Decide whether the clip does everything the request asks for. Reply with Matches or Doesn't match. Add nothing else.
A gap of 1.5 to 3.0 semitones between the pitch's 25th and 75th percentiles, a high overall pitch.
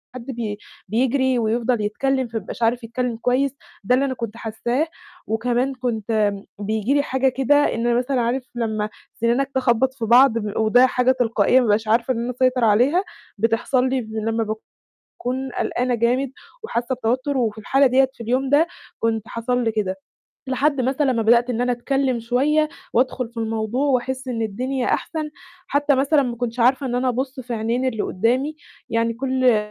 Matches